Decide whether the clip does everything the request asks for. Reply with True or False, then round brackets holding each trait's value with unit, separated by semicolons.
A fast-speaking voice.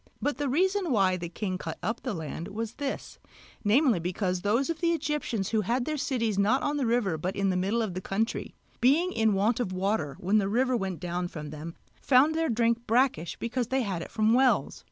True (220 wpm)